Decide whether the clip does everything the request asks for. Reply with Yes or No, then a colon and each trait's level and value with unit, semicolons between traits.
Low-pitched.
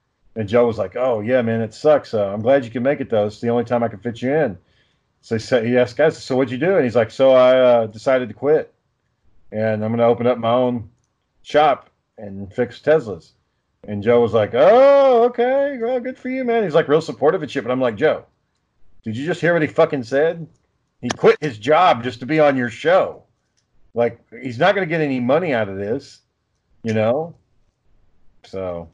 Yes: low, 125 Hz